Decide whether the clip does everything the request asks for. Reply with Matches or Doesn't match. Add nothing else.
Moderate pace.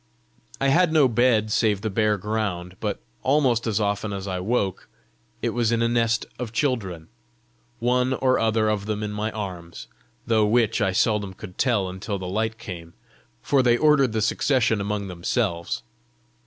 Matches